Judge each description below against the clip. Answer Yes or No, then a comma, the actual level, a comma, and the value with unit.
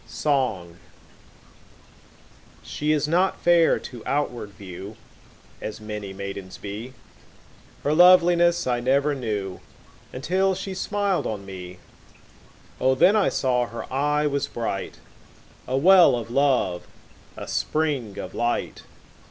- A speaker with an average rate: No, slow, 120 wpm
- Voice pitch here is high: No, low, 130 Hz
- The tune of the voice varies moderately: No, wide, 7.2 semitones